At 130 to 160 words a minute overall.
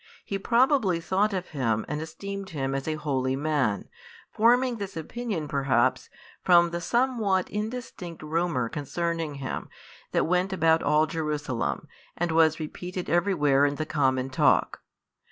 Yes: average, 140 wpm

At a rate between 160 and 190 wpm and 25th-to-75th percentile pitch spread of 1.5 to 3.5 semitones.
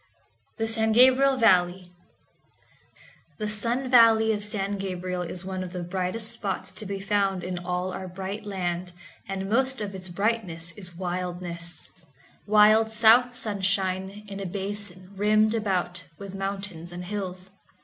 No: average, 140 wpm; average, 2.8 semitones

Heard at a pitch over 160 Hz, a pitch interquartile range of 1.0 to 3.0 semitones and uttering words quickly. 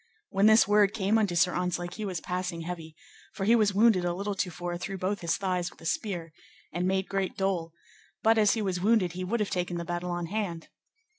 Yes: medium, 185 Hz; average, 2.7 semitones; fast, 230 wpm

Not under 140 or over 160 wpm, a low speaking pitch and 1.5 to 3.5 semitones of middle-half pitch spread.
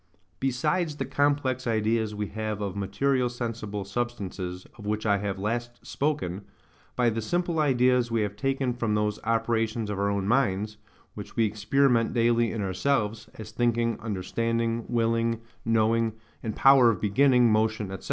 Yes: average, 150 wpm; low, 115 Hz; narrow, 2.6 semitones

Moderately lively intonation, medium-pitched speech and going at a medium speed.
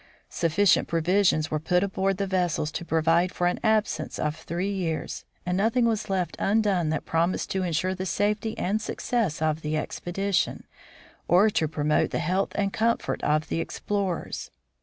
Yes: average, 3.7 semitones; medium, 180 Hz; average, 165 wpm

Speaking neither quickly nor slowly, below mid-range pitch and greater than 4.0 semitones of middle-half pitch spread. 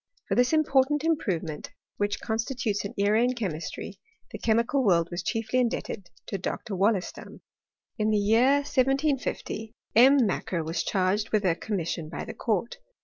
No: average, 150 wpm; high, 220 Hz; average, 4.8 semitones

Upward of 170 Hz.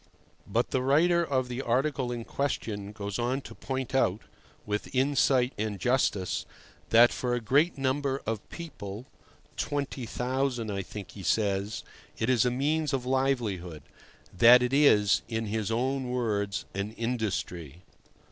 No: low, 120 Hz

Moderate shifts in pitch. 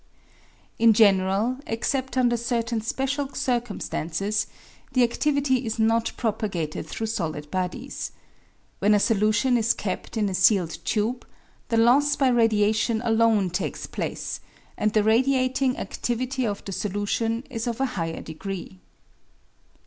Yes: average, 3.3 semitones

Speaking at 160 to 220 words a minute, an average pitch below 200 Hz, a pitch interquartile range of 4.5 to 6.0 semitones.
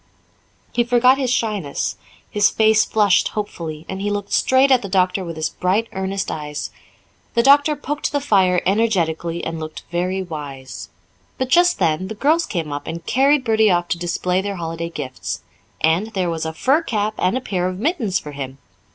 Yes: average, 185 wpm; high, 190 Hz; wide, 5.6 semitones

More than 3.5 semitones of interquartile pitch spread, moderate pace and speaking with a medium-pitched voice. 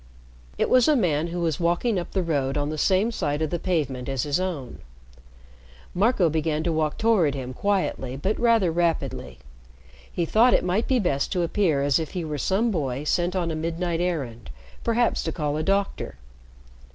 Yes: average, 4.5 semitones; average, 190 wpm; medium, 170 Hz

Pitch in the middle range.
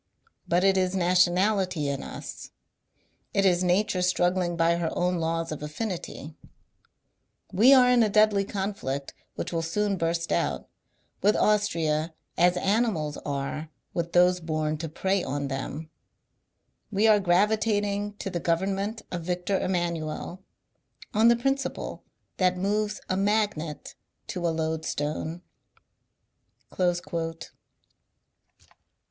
Yes: medium, 180 Hz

